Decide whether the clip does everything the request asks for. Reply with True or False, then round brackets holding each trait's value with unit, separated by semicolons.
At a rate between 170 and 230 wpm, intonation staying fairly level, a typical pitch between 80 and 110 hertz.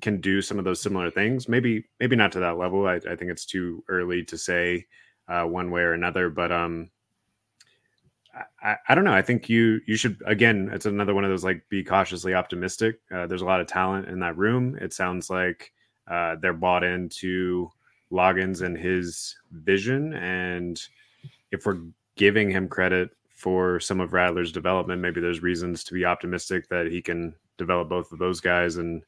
True (190 wpm; 2.1 semitones; 90 Hz)